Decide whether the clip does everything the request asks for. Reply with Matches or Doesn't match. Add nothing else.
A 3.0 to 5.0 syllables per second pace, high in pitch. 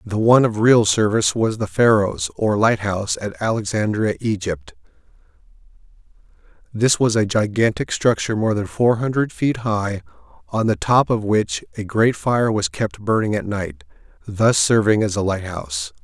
Doesn't match